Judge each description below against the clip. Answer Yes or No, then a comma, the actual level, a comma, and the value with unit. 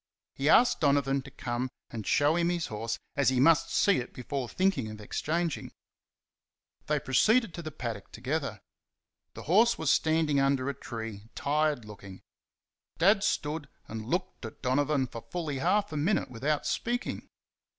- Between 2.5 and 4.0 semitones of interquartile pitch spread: No, average, 4.9 semitones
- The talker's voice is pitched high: No, medium, 140 Hz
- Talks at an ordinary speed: Yes, average, 160 wpm